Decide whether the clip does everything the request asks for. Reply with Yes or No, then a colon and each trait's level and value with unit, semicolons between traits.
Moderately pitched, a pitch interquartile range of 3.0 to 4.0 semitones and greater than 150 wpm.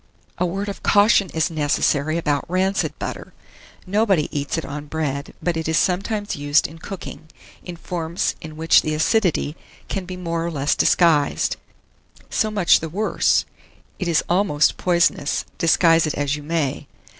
Yes: medium, 165 Hz; average, 3.4 semitones; average, 160 wpm